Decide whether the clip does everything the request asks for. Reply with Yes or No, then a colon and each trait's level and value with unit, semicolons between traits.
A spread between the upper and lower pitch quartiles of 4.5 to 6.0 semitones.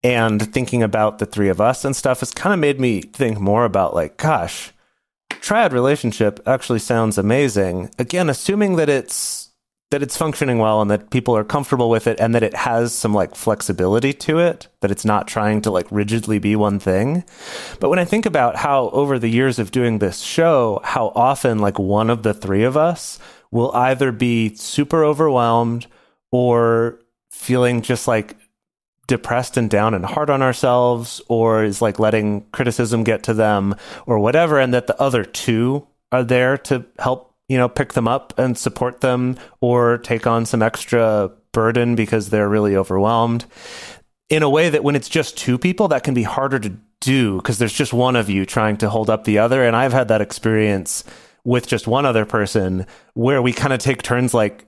No: average, 3.3 semitones